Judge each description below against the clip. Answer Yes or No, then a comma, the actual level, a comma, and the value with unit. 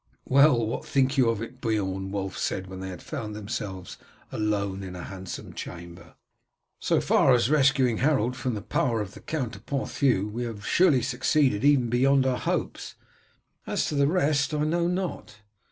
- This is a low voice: Yes, low, 120 Hz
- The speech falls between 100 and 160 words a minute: No, average, 175 wpm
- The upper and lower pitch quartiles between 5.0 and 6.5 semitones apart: Yes, wide, 5.4 semitones